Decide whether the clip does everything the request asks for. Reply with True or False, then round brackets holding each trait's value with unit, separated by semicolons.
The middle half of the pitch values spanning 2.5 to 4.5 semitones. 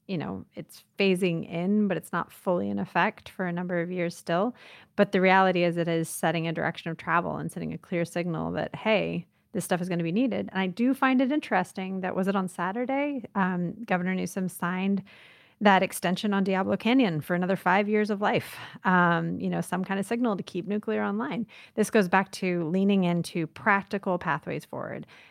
True (2.9 semitones)